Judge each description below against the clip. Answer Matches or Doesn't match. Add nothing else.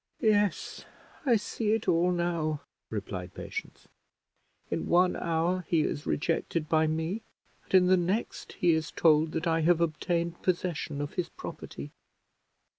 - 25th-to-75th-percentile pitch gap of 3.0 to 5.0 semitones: Doesn't match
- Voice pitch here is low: Doesn't match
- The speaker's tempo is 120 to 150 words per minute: Matches